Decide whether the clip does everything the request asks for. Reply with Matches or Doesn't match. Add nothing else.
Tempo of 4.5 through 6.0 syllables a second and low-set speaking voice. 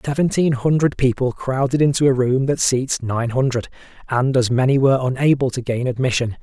Matches